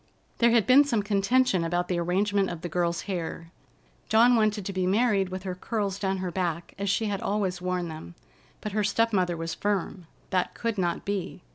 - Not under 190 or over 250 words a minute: Yes, fast, 205 wpm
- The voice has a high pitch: Yes, high, 195 Hz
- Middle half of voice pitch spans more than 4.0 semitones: No, average, 3.0 semitones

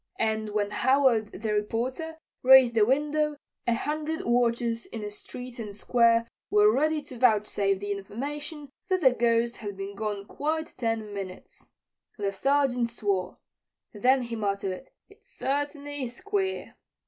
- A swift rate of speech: No, average, 145 wpm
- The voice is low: No, high, 235 Hz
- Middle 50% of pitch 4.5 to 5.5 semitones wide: Yes, average, 5.2 semitones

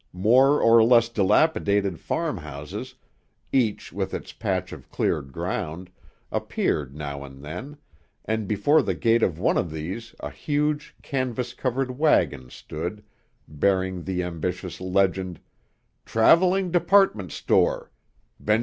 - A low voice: Yes, low, 100 Hz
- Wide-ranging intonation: Yes, wide, 7.0 semitones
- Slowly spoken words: Yes, slow, 125 wpm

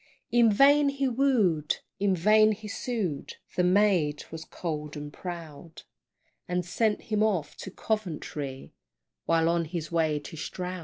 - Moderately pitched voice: Yes, medium, 180 Hz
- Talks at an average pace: Yes, average, 145 wpm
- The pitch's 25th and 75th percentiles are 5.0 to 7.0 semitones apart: Yes, average, 5.3 semitones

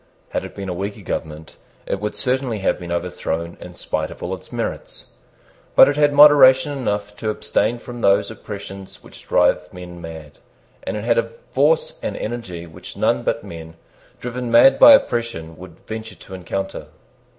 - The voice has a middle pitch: No, low, 105 Hz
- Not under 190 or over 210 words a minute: No, average, 175 wpm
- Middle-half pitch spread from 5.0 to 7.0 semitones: Yes, wide, 5.6 semitones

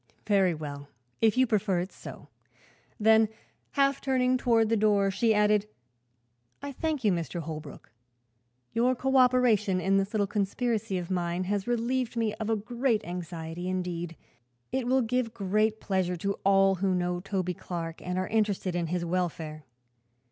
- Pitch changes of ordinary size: Yes, average, 4.2 semitones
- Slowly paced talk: No, average, 155 wpm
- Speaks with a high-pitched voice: Yes, high, 200 Hz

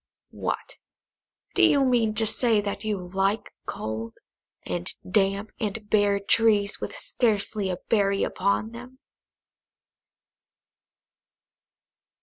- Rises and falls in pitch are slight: Yes, narrow, 2.3 semitones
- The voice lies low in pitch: No, high, 205 Hz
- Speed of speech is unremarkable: No, slow, 105 wpm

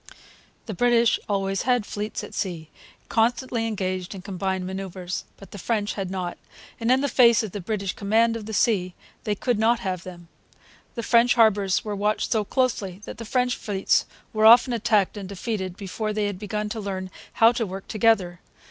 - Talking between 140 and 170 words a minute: No, average, 185 wpm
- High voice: Yes, high, 210 Hz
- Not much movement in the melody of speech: No, average, 3.2 semitones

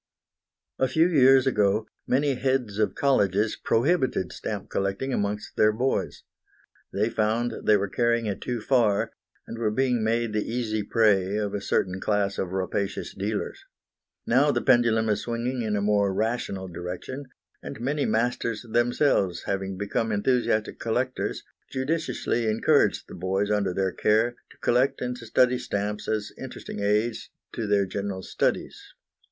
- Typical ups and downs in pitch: Yes, average, 3.4 semitones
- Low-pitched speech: Yes, low, 110 Hz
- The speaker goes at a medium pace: Yes, average, 150 wpm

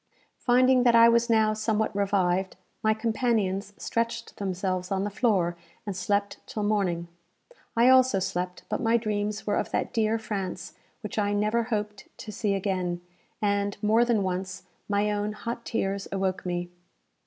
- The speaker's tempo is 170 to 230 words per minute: No, average, 160 wpm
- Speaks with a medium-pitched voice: No, high, 205 Hz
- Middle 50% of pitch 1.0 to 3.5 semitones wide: Yes, average, 2.8 semitones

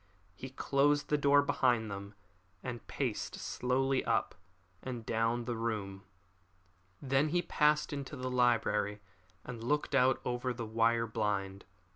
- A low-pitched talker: Yes, low, 120 Hz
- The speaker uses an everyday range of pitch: Yes, average, 3.3 semitones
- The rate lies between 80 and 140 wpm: Yes, slow, 135 wpm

